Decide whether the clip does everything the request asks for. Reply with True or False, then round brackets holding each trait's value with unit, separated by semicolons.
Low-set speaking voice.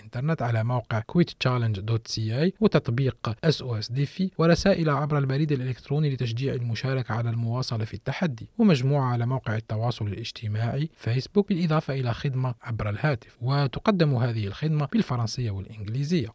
True (130 Hz)